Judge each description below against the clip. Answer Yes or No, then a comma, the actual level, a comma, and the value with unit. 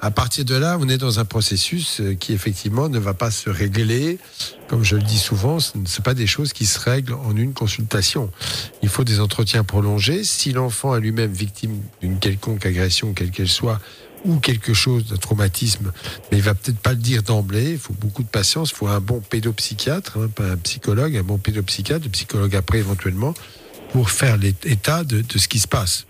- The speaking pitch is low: Yes, low, 110 Hz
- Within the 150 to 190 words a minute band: No, average, 215 wpm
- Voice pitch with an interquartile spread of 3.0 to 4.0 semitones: Yes, average, 3.5 semitones